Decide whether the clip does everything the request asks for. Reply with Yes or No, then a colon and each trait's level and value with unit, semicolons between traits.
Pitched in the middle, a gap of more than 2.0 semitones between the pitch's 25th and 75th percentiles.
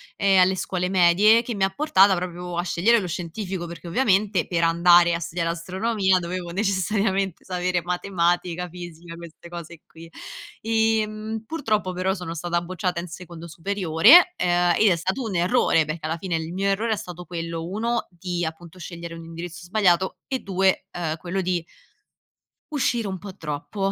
Yes: medium, 180 Hz; narrow, 2.5 semitones